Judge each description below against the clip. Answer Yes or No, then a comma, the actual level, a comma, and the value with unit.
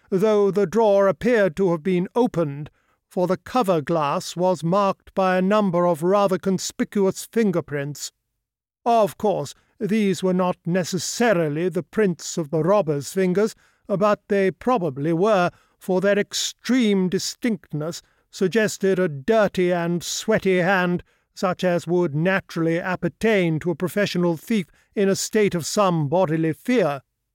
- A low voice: No, medium, 185 Hz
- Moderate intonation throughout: Yes, average, 3.0 semitones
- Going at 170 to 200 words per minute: No, average, 140 wpm